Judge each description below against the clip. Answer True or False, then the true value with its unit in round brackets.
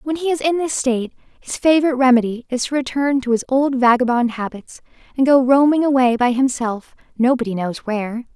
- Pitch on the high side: True (255 Hz)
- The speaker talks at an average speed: True (185 wpm)